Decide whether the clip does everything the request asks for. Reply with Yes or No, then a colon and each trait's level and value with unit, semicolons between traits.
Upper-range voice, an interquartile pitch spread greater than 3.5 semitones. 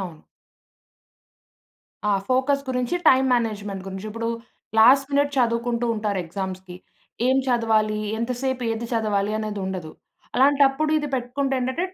Yes: high, 235 Hz; average, 4.0 semitones